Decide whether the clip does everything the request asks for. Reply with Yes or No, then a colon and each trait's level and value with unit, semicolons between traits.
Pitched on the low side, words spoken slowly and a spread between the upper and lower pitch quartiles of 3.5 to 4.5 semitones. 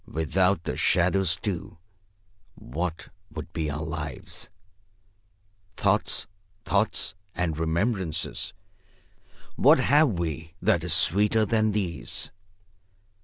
Yes: very low, 90 Hz; slow, 95 wpm; average, 3.9 semitones